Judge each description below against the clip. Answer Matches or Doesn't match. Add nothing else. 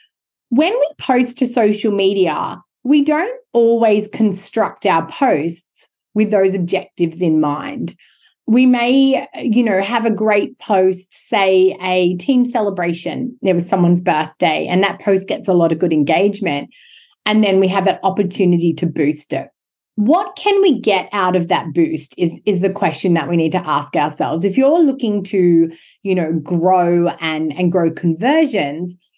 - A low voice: Doesn't match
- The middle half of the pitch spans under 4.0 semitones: Doesn't match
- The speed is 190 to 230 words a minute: Doesn't match